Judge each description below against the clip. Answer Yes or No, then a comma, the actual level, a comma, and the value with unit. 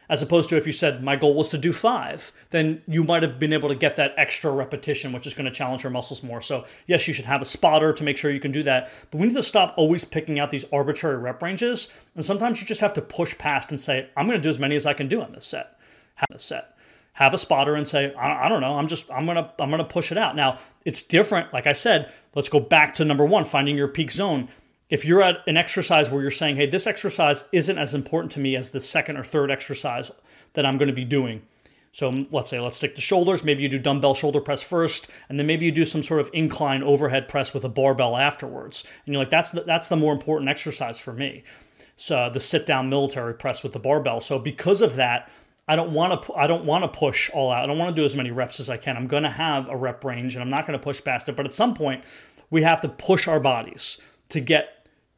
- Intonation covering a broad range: No, average, 2.9 semitones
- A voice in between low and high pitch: Yes, medium, 145 Hz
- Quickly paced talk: Yes, fast, 270 wpm